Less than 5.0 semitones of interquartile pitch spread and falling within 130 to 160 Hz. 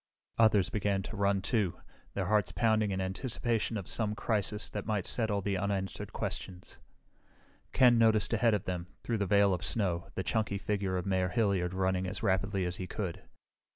No: narrow, 2.5 semitones; low, 100 Hz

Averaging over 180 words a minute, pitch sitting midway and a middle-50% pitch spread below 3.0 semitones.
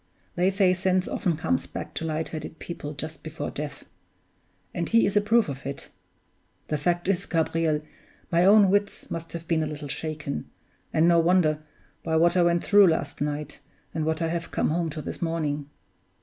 Yes: average, 190 wpm; medium, 165 Hz; narrow, 2.6 semitones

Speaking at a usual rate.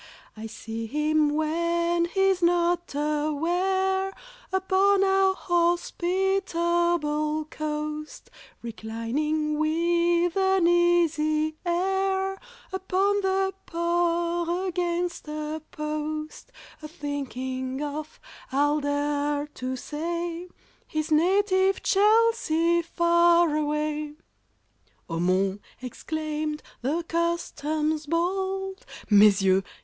No: slow, 85 wpm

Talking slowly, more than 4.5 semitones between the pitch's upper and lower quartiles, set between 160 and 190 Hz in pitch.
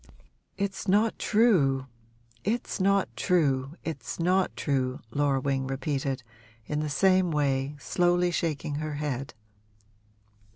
No: slow, 115 wpm; average, 5.1 semitones; medium, 150 Hz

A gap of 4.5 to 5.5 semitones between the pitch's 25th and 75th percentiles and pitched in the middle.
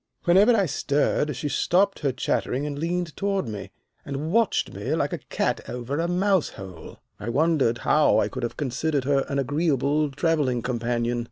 Yes: average, 5.0 semitones; medium, 145 Hz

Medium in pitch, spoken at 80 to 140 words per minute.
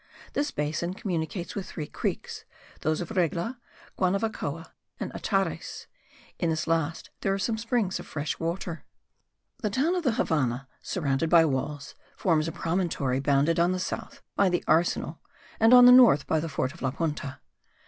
No: medium, 165 Hz; average, 170 wpm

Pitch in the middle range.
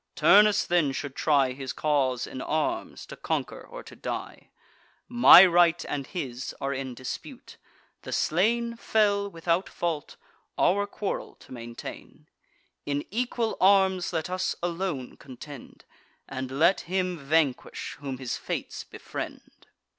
Yes: medium, 165 Hz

